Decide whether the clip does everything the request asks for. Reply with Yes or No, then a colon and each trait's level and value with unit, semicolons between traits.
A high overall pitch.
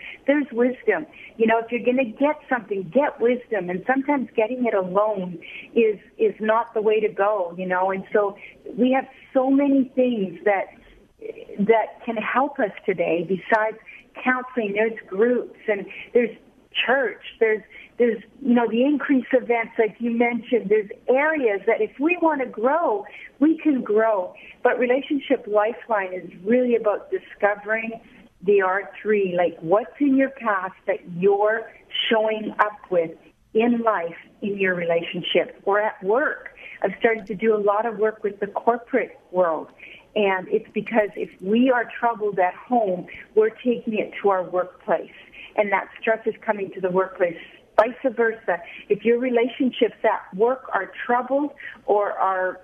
Yes: high, 225 Hz